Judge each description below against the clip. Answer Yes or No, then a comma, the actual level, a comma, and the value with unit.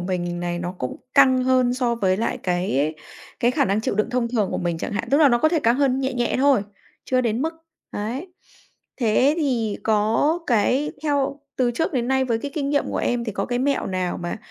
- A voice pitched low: No, high, 245 Hz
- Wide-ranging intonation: No, average, 4.6 semitones